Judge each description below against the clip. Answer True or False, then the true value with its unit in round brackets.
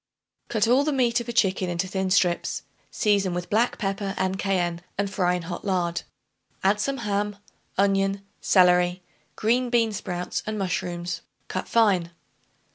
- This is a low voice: False (195 Hz)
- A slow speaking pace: False (155 wpm)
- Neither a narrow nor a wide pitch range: True (3.0 semitones)